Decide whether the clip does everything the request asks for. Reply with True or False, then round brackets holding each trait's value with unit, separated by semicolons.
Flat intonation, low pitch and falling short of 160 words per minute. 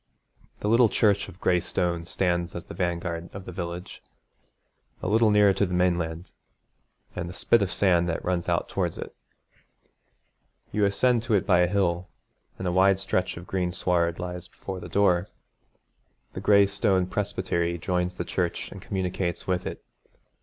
False (2.2 semitones; 90 Hz; 170 wpm)